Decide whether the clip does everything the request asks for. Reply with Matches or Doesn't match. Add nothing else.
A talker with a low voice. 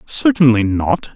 Matches